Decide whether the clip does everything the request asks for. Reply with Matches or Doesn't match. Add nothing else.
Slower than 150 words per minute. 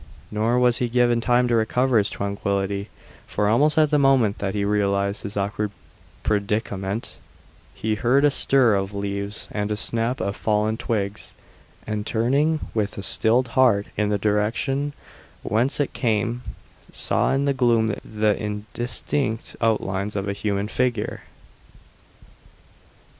Matches